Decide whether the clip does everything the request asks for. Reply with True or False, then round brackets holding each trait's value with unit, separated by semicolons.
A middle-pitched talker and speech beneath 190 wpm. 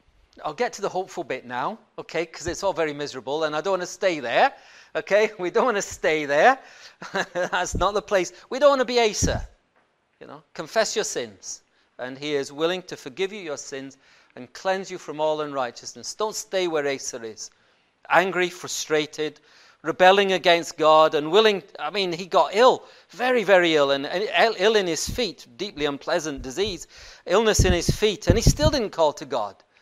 False (175 Hz; 195 wpm)